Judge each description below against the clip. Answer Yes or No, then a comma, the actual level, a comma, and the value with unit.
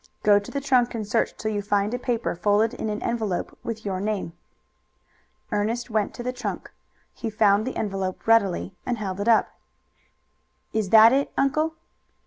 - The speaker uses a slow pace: No, average, 175 wpm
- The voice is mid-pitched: No, high, 220 Hz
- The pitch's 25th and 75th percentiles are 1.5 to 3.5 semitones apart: Yes, average, 2.8 semitones